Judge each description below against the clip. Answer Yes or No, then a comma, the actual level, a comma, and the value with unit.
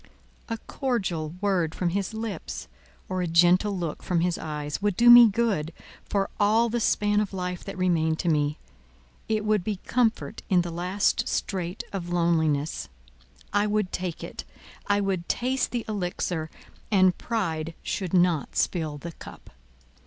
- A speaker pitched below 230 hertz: Yes, medium, 185 Hz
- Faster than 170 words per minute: No, average, 155 wpm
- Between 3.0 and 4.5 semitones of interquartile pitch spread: Yes, average, 3.8 semitones